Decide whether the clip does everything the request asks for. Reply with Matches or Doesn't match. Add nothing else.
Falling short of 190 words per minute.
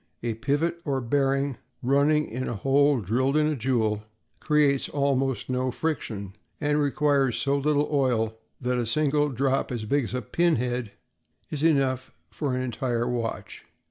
Matches